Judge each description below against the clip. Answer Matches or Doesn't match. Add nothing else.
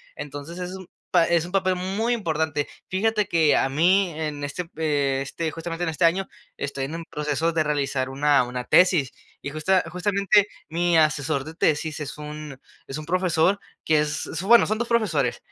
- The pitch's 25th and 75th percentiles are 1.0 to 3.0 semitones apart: Doesn't match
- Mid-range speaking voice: Matches